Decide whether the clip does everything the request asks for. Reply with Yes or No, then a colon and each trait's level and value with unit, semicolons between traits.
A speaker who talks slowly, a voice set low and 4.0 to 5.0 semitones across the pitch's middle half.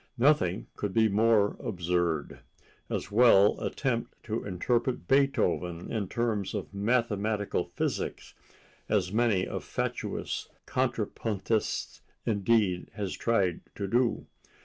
No: slow, 100 wpm; low, 105 Hz; average, 3.6 semitones